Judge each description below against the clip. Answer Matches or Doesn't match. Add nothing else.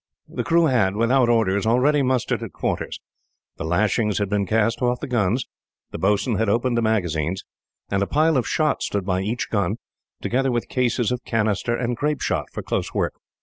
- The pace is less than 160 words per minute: Doesn't match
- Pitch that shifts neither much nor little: Matches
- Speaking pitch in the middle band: Doesn't match